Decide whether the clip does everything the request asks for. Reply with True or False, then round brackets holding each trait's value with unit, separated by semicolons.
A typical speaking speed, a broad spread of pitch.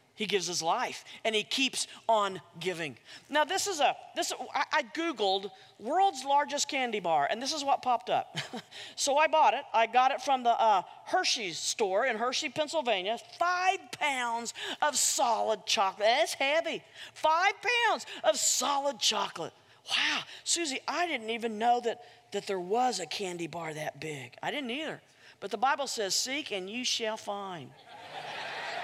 True (170 wpm; 7.2 semitones)